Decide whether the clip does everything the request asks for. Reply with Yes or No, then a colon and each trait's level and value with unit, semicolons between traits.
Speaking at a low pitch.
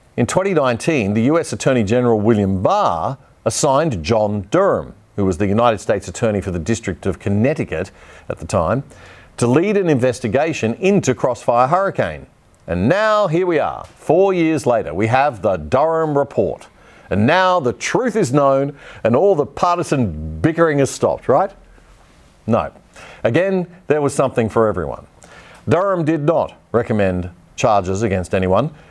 Yes: low, 125 Hz